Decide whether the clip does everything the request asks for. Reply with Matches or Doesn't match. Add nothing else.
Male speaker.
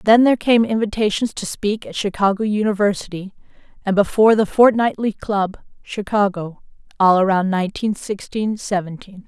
Doesn't match